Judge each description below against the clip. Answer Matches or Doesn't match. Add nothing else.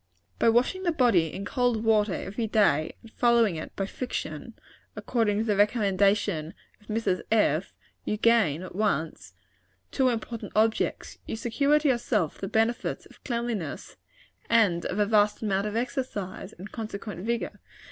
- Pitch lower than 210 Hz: Doesn't match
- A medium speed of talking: Matches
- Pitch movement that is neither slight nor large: Matches